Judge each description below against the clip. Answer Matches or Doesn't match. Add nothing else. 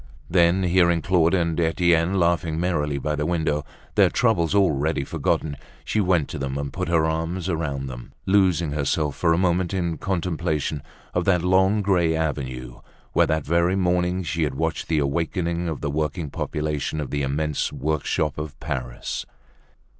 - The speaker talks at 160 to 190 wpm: Matches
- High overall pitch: Doesn't match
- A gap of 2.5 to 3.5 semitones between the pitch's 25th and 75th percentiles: Matches